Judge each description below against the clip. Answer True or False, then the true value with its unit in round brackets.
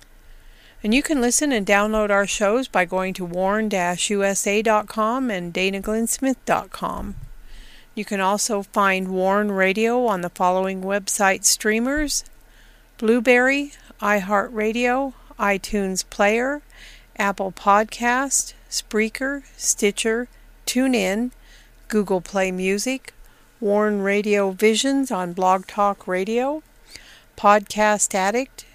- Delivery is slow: True (95 wpm)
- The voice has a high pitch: True (210 Hz)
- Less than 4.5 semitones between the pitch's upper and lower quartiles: True (3.8 semitones)